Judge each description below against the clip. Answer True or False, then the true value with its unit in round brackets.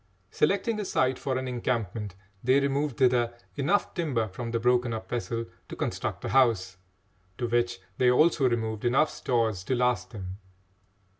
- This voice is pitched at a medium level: False (120 Hz)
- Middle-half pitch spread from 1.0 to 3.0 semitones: True (2.6 semitones)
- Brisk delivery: False (160 wpm)